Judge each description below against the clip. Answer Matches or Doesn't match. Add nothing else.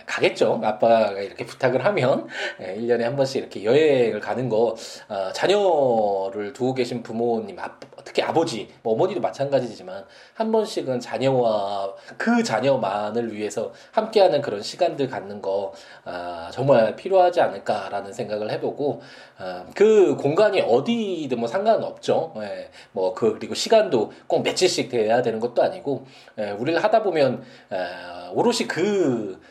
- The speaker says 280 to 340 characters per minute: Matches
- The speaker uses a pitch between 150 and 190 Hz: Doesn't match